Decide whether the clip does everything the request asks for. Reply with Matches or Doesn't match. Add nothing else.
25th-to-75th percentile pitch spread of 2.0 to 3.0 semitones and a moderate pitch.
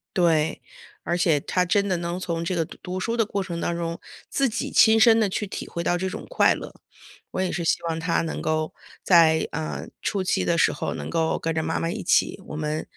Matches